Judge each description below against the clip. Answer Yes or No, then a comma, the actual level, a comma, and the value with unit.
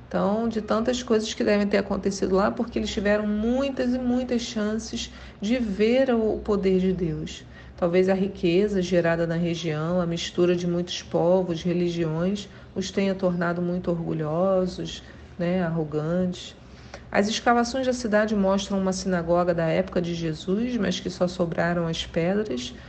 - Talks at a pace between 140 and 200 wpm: Yes, average, 150 wpm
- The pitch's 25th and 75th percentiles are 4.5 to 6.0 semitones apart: No, average, 3.5 semitones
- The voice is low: No, medium, 185 Hz